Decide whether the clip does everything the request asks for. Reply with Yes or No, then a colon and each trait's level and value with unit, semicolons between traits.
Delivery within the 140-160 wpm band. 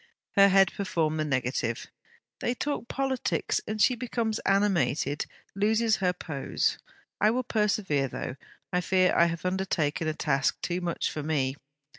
Yes: average, 150 wpm